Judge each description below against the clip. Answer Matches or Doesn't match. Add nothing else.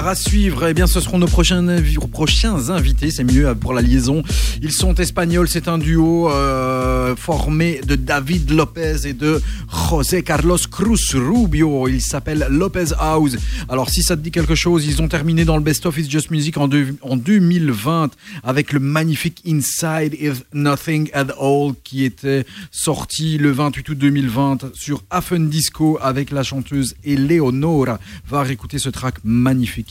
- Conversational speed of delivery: Matches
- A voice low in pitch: Doesn't match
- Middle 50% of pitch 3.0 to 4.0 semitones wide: Matches